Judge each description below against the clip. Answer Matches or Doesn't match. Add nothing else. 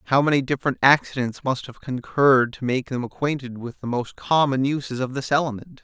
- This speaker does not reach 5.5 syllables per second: Doesn't match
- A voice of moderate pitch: Doesn't match